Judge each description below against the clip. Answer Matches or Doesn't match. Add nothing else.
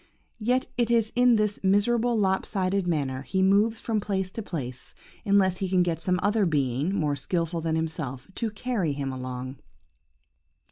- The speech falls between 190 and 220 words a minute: Doesn't match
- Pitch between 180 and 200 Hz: Matches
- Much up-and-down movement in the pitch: Matches